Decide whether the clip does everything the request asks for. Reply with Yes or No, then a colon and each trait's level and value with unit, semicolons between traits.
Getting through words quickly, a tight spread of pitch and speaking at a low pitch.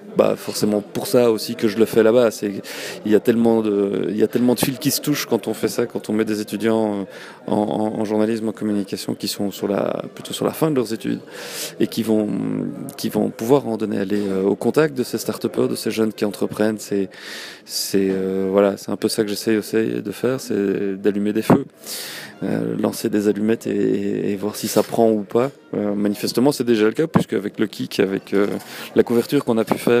Yes: fast, 230 wpm; narrow, 2.3 semitones; low, 110 Hz